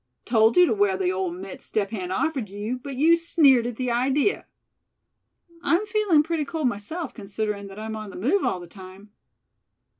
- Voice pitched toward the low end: No, high, 225 Hz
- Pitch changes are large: Yes, wide, 7.1 semitones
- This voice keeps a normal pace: Yes, average, 185 wpm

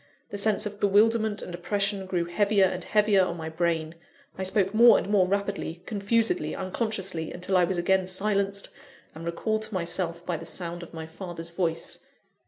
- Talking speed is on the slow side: No, average, 180 wpm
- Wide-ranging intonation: No, average, 3.0 semitones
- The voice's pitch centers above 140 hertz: Yes, high, 190 Hz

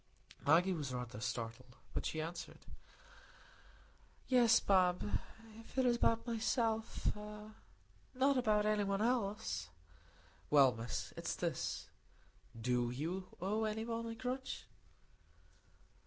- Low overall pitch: No, high, 200 Hz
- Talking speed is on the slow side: Yes, slow, 105 wpm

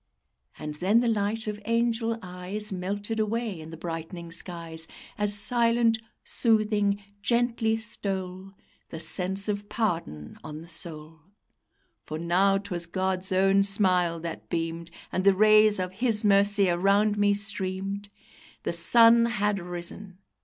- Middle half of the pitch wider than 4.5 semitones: No, average, 3.4 semitones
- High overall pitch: Yes, high, 195 Hz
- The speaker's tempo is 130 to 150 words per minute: Yes, slow, 135 wpm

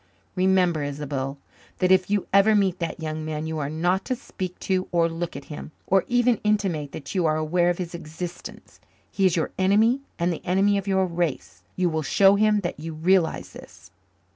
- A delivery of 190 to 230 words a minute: Yes, average, 200 wpm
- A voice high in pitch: No, medium, 175 Hz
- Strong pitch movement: No, average, 3.4 semitones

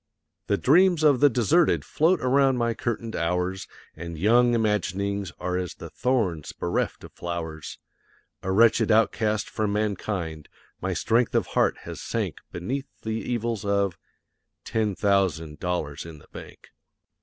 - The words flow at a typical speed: Yes, average, 145 wpm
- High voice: No, low, 105 Hz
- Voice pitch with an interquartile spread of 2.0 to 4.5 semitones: No, average, 4.9 semitones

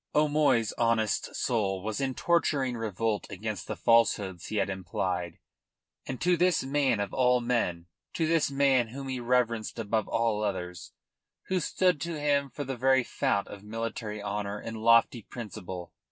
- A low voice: Yes, low, 115 Hz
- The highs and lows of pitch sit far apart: No, average, 4.5 semitones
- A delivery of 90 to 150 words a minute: No, average, 160 wpm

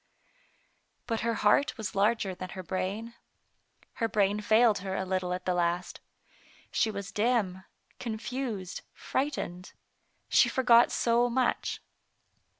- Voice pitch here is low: No, high, 210 Hz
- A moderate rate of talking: No, slow, 125 wpm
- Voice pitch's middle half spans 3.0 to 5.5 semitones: Yes, average, 3.8 semitones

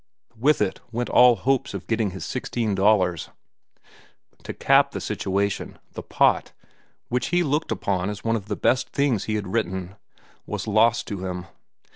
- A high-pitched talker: No, low, 110 Hz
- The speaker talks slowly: No, average, 165 wpm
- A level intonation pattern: No, average, 4.1 semitones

